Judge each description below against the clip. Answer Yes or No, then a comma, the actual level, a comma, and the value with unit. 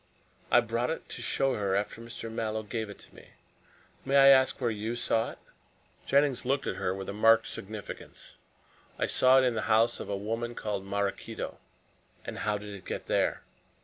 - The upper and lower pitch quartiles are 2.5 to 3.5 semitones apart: Yes, average, 3.0 semitones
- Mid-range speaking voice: No, low, 115 Hz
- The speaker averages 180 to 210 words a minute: Yes, average, 190 wpm